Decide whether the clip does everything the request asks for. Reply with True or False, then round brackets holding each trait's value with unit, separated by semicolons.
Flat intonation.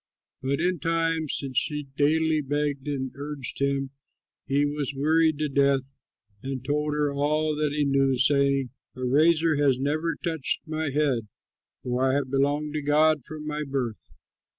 True (2.0 semitones)